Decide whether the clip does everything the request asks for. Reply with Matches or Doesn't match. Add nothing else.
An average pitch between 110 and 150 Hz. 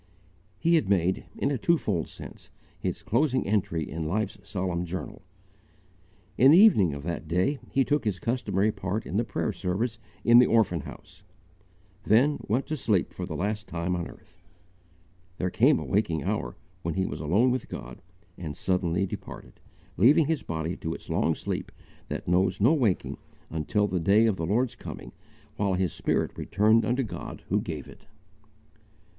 Doesn't match